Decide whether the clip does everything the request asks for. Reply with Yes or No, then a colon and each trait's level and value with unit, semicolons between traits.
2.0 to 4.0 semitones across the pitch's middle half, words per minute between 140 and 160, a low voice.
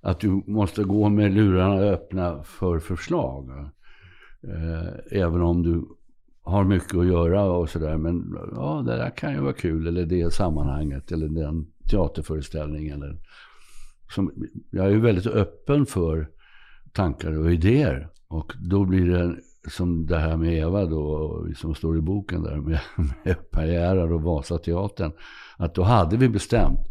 Yes: average, 3.3 semitones; average, 150 wpm; very low, 85 Hz